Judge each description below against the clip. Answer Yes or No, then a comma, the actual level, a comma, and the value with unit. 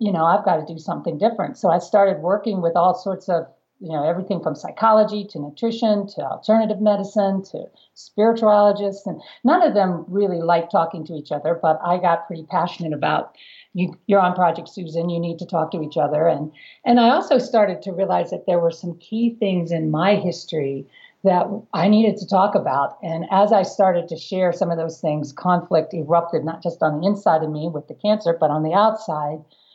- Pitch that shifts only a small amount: No, average, 3.8 semitones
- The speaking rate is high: Yes, fast, 210 wpm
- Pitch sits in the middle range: Yes, medium, 180 Hz